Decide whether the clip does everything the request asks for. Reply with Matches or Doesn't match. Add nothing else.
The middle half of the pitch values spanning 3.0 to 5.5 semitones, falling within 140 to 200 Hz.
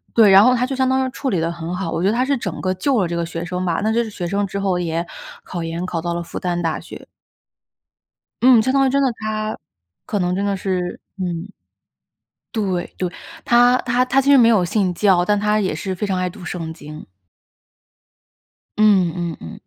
Matches